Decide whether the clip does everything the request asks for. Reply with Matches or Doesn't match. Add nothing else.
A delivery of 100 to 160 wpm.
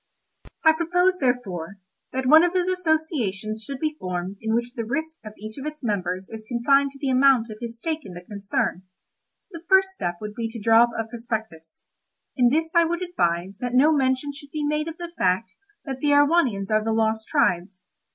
Doesn't match